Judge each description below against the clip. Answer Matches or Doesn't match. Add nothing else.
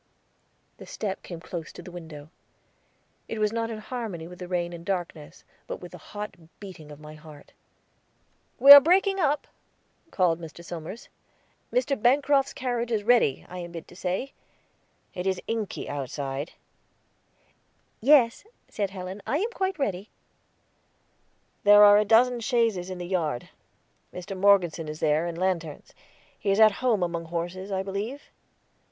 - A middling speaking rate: Matches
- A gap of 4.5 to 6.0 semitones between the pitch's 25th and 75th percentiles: Matches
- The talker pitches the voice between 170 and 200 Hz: Matches